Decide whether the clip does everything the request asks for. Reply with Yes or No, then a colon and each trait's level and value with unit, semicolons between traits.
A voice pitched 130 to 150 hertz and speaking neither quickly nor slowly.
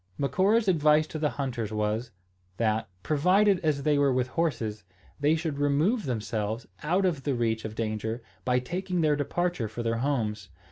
Yes: medium, 140 Hz; average, 170 wpm